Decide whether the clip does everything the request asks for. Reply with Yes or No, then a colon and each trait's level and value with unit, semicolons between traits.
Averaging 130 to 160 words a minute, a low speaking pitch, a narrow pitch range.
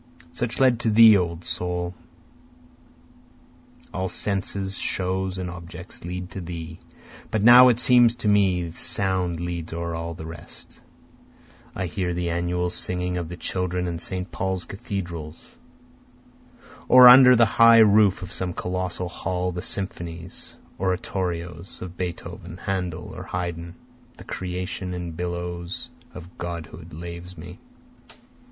Yes: slow, 135 wpm; very low, 90 Hz; narrow, 1.8 semitones